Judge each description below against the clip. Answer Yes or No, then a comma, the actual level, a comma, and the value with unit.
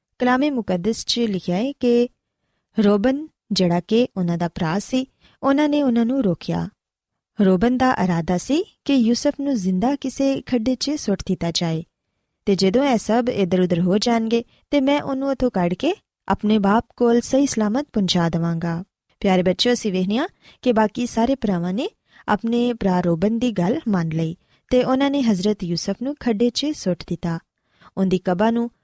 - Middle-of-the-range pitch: No, high, 225 Hz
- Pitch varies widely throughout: Yes, wide, 5.7 semitones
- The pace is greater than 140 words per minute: Yes, fast, 165 wpm